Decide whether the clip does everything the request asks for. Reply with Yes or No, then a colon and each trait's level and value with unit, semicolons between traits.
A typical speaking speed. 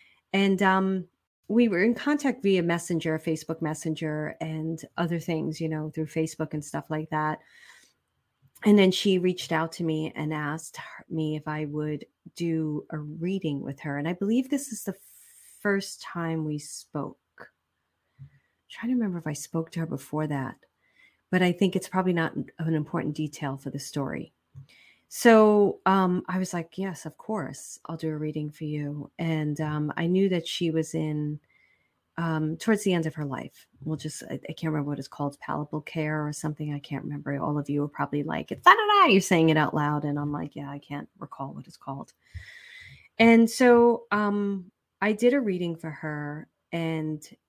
Yes: average, 190 wpm